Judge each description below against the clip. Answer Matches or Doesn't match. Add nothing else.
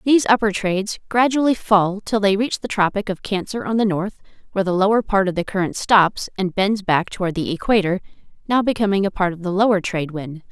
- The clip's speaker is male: Doesn't match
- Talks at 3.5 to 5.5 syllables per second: Doesn't match